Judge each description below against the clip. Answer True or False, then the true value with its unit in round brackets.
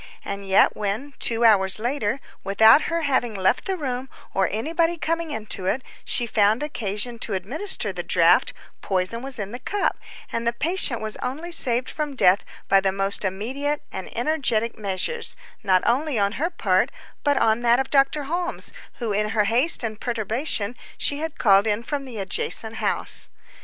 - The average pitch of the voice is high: True (235 Hz)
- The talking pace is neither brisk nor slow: True (175 wpm)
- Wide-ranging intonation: True (5.9 semitones)